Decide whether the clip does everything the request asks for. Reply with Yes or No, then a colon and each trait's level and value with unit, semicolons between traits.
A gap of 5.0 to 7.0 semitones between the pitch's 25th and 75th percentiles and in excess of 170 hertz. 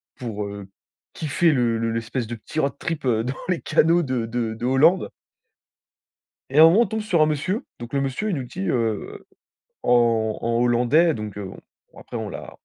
No: wide, 5.6 semitones; low, 125 Hz